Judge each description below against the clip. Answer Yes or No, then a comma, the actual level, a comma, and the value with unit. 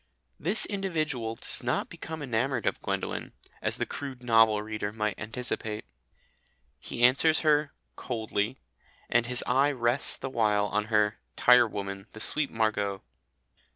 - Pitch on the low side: Yes, low, 120 Hz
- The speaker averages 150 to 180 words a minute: No, slow, 135 wpm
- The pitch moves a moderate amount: Yes, average, 4.2 semitones